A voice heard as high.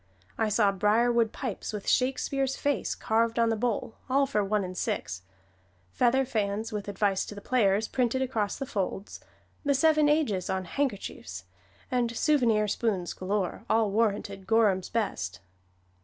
Yes: high, 220 Hz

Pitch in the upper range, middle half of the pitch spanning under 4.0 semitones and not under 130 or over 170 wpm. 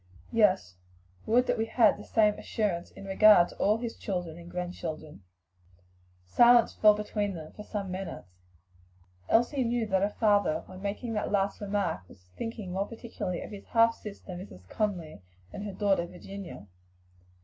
Yes: high, 200 Hz; average, 3.3 semitones; average, 160 wpm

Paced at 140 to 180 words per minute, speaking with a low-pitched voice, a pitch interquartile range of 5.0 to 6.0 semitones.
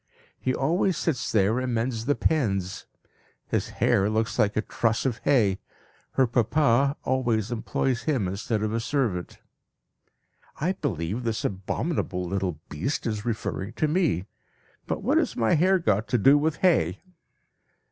Yes: average, 150 wpm; low, 115 Hz; wide, 5.6 semitones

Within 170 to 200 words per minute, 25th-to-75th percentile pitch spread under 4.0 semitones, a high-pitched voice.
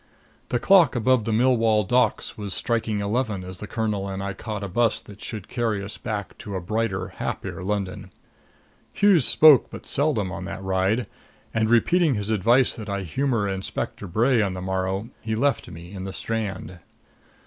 No: average, 180 wpm; average, 3.5 semitones; low, 105 Hz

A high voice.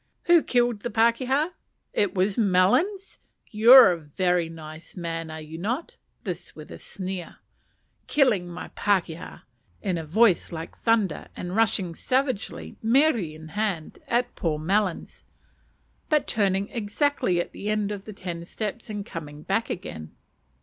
Yes: high, 200 Hz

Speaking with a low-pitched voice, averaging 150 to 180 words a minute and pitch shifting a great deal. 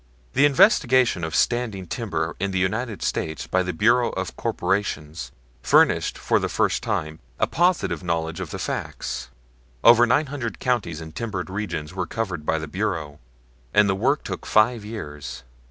Yes: very low, 95 Hz; average, 165 wpm; wide, 6.4 semitones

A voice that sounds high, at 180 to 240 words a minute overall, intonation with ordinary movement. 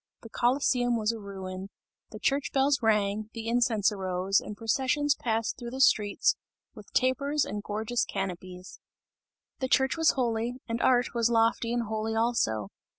No: high, 230 Hz; average, 155 wpm; average, 3.2 semitones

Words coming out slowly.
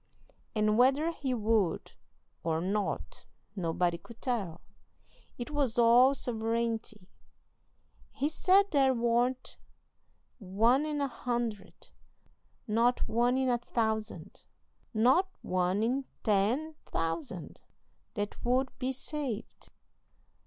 Yes: slow, 105 wpm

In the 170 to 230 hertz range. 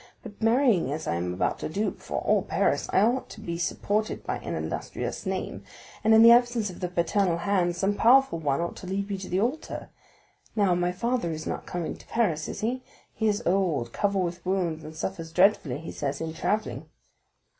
Yes: high, 190 Hz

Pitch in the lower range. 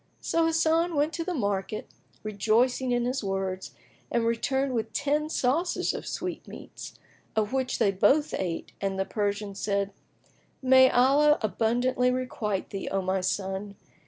No: high, 235 Hz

